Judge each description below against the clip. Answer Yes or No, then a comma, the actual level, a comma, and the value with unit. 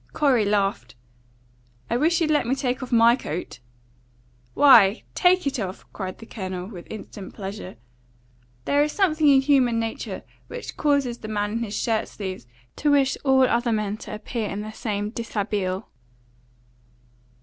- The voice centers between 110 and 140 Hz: No, high, 230 Hz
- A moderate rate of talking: Yes, average, 160 wpm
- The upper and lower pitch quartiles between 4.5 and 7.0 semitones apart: Yes, average, 4.9 semitones